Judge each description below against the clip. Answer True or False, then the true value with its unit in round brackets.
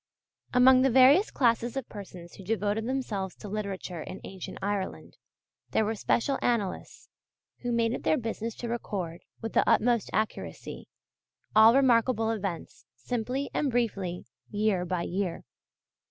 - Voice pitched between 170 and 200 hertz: False (220 Hz)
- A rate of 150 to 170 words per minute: False (140 wpm)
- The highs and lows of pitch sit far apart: False (3.9 semitones)